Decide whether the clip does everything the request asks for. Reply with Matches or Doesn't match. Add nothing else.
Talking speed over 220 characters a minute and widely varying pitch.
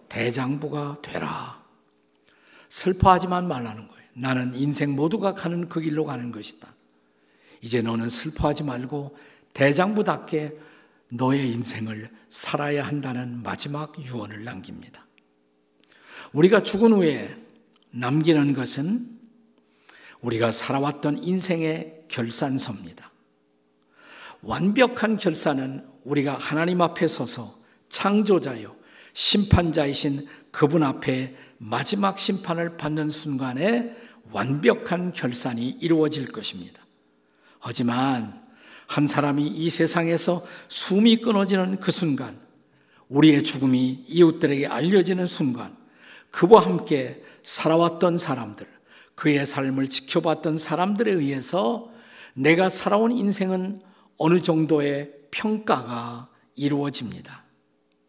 Matches